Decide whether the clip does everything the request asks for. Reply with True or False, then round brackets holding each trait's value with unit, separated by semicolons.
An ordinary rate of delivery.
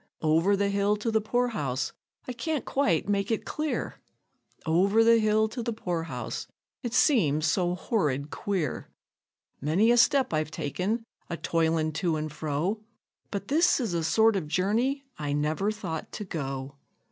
True (165 wpm)